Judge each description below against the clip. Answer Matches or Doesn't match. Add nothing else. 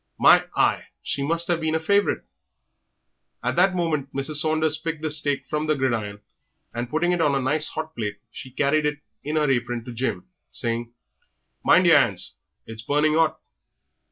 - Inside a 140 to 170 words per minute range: Doesn't match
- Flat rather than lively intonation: Doesn't match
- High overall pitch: Doesn't match